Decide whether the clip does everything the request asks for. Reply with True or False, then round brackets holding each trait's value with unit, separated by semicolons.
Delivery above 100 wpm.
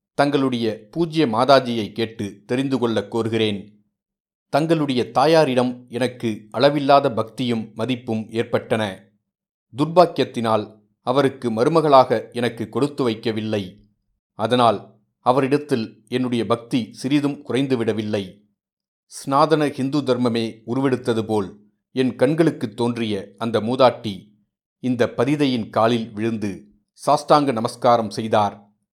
False (90 wpm)